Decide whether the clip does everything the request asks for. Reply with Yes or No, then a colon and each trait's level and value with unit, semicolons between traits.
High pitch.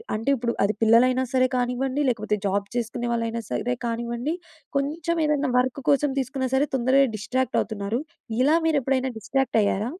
Yes: very high, 250 Hz